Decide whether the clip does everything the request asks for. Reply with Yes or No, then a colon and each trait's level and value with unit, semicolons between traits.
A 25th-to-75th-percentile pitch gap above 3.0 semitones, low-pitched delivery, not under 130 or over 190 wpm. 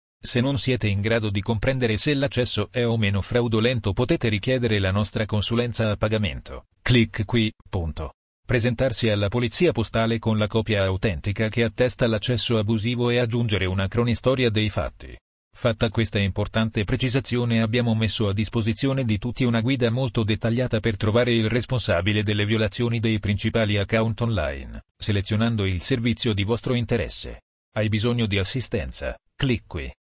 No: narrow, 2.4 semitones; low, 115 Hz; average, 155 wpm